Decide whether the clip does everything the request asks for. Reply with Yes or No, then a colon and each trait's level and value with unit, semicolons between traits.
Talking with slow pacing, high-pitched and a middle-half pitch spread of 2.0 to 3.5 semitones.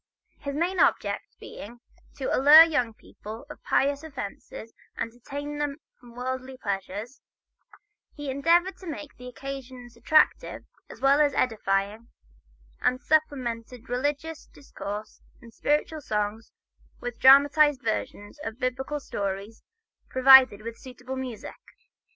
No: slow, 125 wpm; very high, 260 Hz; average, 4.1 semitones